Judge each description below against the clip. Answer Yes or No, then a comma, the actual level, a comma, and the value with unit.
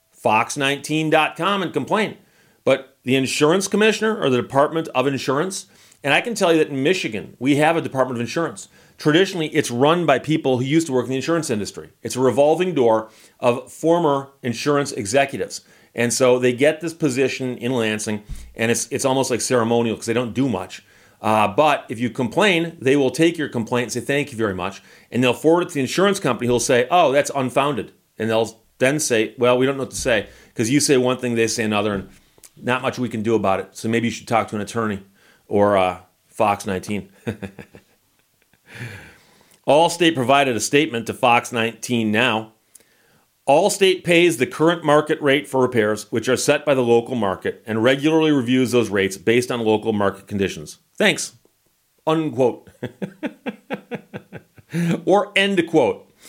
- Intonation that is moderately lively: Yes, average, 5.0 semitones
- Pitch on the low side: Yes, low, 130 Hz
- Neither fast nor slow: Yes, average, 185 wpm